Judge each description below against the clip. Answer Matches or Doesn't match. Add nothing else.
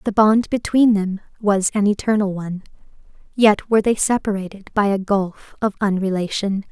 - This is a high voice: Matches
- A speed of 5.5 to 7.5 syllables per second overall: Doesn't match